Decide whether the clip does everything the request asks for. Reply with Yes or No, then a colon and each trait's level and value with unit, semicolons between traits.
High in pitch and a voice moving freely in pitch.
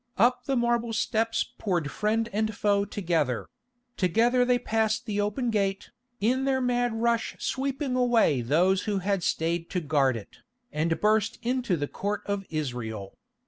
Yes: high, 210 Hz; wide, 5.7 semitones